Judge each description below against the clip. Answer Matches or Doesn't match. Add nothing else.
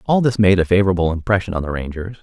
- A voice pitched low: Matches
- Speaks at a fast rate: Matches